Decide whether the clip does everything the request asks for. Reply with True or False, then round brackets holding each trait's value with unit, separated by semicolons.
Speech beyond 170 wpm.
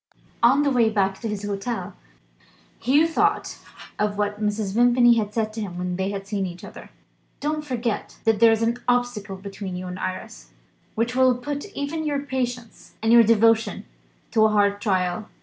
True (185 wpm)